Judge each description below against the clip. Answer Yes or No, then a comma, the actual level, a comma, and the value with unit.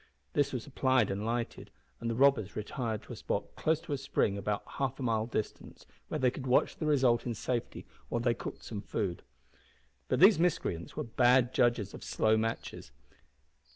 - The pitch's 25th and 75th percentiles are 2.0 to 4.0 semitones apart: Yes, average, 3.2 semitones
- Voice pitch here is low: Yes, low, 120 Hz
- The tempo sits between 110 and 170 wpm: No, average, 190 wpm